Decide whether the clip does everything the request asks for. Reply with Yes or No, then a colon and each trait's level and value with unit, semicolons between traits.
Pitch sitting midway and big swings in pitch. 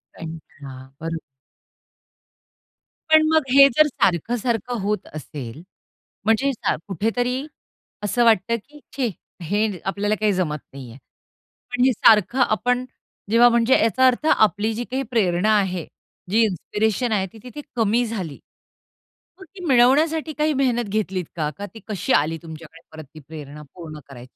No: high, 215 Hz; wide, 6.7 semitones